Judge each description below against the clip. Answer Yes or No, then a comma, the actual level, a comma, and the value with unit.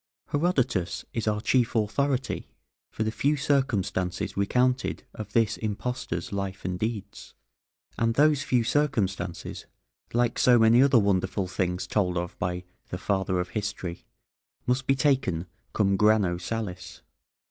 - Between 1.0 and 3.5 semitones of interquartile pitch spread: No, average, 5.1 semitones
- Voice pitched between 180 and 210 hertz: No, low, 110 Hz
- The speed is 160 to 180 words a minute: No, slow, 135 wpm